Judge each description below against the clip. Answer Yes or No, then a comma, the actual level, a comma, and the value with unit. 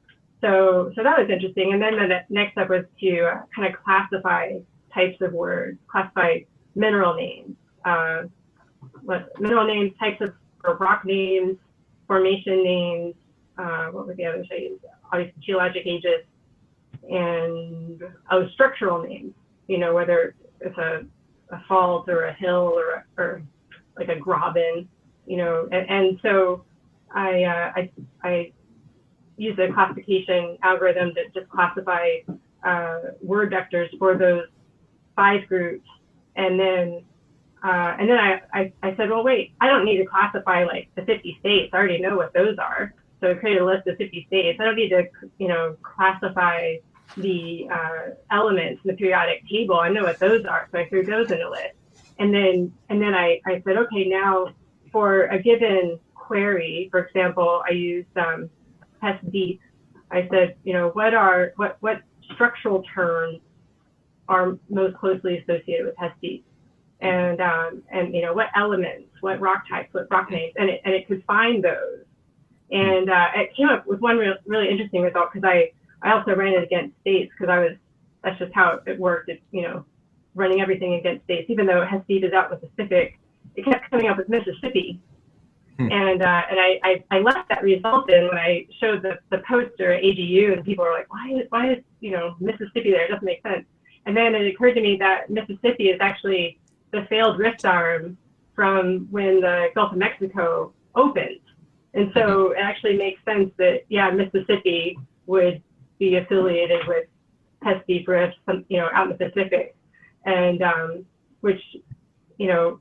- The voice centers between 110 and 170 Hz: No, medium, 185 Hz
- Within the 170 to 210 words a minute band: Yes, average, 175 wpm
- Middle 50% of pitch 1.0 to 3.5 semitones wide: Yes, narrow, 2.4 semitones